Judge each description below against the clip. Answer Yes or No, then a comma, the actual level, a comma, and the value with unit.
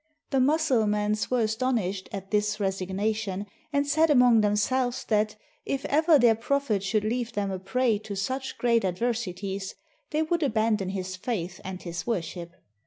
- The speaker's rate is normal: Yes, average, 165 wpm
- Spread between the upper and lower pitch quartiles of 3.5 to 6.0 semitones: Yes, average, 4.4 semitones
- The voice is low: No, high, 215 Hz